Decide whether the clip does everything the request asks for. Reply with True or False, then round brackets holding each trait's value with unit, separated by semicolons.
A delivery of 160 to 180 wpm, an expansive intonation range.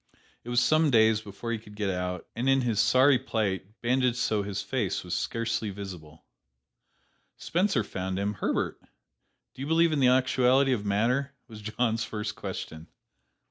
False (165 wpm; 4.2 semitones)